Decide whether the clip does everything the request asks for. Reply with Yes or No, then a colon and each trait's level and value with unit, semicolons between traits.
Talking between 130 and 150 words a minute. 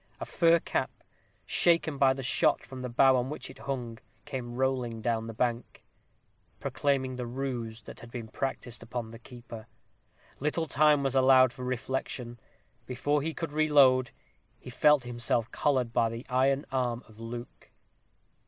No: average, 160 wpm